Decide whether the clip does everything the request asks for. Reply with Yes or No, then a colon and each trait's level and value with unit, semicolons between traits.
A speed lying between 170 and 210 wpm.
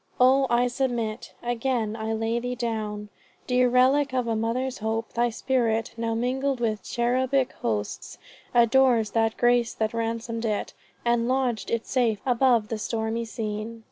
No: average, 150 wpm